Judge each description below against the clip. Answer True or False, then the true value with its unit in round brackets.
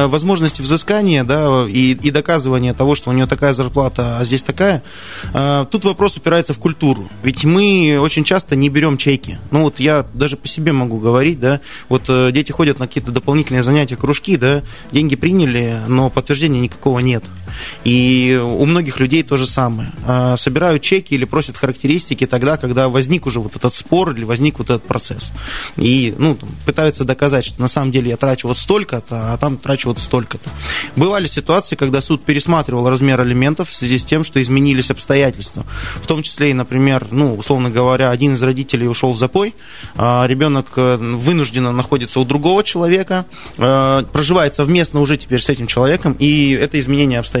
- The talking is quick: True (175 wpm)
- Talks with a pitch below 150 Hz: True (135 Hz)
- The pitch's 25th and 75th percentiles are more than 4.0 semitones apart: False (3.0 semitones)